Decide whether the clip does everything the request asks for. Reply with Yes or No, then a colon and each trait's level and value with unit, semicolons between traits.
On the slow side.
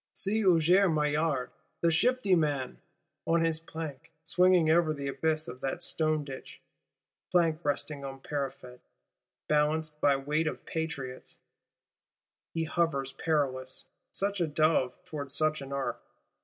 Yes: slow, 130 wpm